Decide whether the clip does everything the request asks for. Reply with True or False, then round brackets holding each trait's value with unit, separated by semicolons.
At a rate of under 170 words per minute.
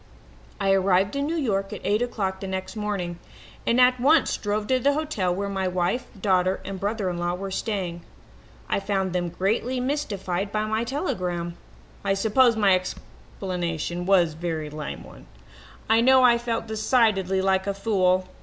False (175 wpm)